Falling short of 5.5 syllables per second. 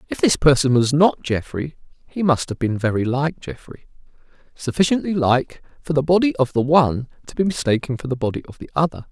No: 5.7 syllables/s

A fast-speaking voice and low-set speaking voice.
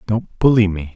No: average, 190 wpm; low, 105 Hz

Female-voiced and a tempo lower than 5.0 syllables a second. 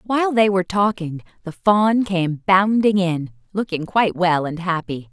Yes: female; 4.6 syllables/s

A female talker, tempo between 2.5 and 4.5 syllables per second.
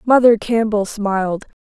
Yes: female; 4.4 syllables/s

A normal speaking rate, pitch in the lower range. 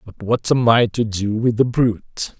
No: fast, 225 wpm; low, 115 Hz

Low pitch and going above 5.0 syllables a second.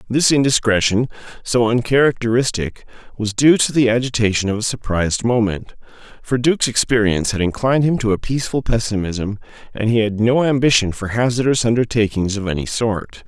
Yes: low, 115 Hz; 5.7 syllables/s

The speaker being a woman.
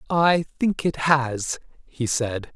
No: male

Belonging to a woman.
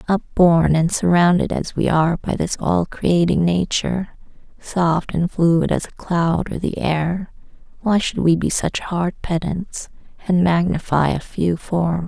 Yes: female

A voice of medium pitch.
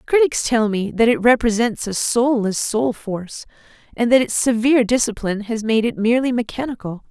No: high, 230 Hz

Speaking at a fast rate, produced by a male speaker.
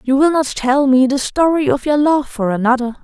No: fast, 235 wpm; female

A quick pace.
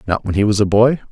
Yes: fast, 325 wpm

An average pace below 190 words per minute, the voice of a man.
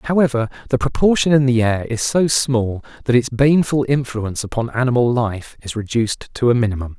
Yes: average, 180 wpm; male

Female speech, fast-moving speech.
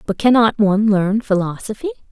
No: female; average, 140 wpm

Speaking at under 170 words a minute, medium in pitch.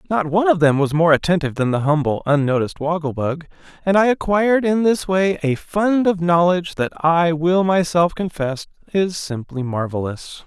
No: average, 180 wpm; medium, 165 Hz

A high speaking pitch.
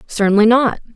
Yes: high, 225 Hz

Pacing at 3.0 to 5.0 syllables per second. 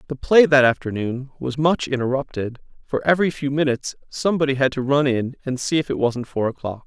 No: 5.8 syllables/s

